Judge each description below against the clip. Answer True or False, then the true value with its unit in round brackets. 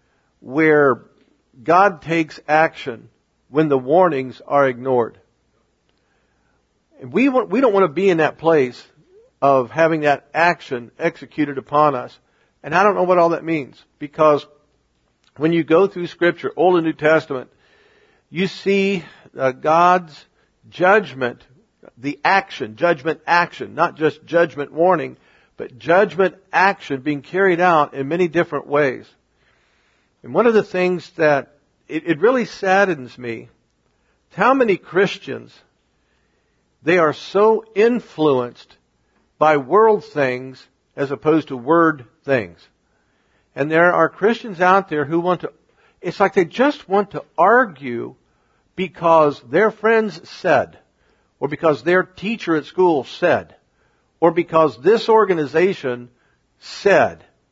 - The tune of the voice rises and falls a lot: False (4.7 semitones)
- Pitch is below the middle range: False (160 Hz)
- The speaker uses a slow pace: True (130 wpm)